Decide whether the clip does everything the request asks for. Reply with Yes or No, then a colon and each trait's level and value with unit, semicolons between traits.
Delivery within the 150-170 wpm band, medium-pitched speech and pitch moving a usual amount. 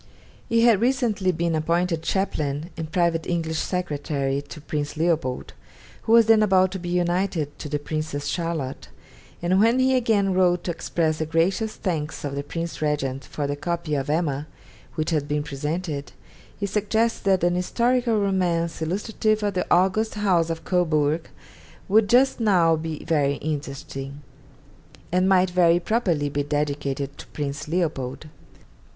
Yes: average, 155 wpm; medium, 170 Hz; average, 4.3 semitones